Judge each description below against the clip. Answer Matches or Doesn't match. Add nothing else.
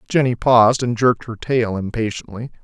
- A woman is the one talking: Doesn't match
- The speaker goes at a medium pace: Matches